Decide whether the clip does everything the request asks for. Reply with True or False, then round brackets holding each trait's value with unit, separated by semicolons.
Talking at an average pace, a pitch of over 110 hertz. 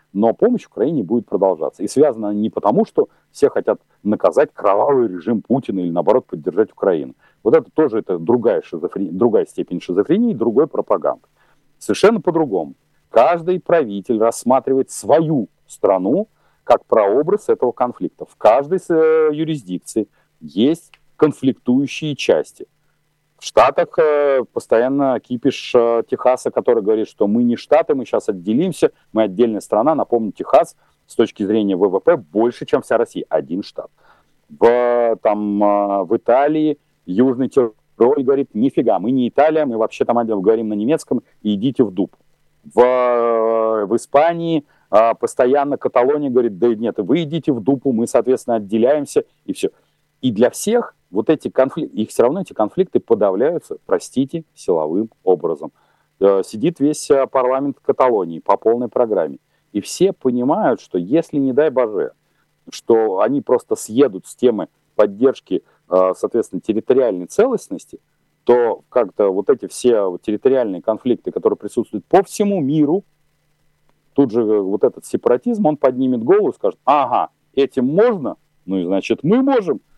True (145 wpm; 140 Hz)